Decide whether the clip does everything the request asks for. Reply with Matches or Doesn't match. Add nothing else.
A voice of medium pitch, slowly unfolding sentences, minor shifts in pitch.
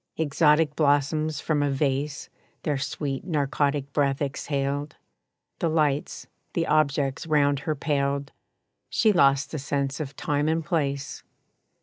Matches